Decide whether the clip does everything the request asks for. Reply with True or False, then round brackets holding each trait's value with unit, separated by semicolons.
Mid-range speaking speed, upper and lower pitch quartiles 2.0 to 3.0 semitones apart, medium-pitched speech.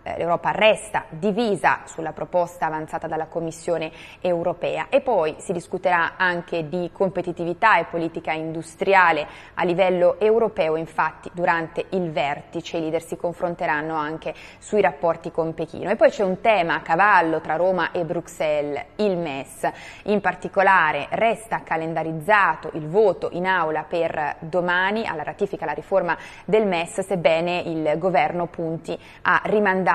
True (140 wpm; 2.7 semitones; 175 Hz)